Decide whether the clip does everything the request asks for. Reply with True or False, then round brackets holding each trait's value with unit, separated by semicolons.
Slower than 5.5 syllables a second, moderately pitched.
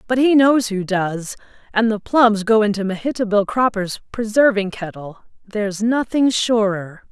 False (4.5 syllables/s; 215 Hz)